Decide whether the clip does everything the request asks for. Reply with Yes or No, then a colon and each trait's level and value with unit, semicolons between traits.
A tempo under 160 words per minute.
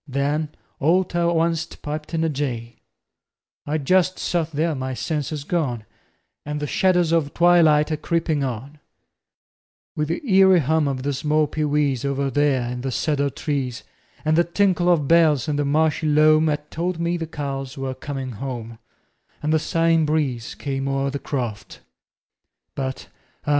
No: average, 170 wpm